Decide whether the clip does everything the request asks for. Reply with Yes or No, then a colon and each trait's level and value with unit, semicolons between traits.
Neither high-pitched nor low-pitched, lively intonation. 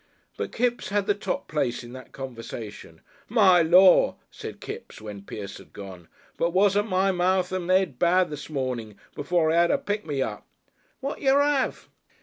Yes: medium, 175 Hz; wide, 7.2 semitones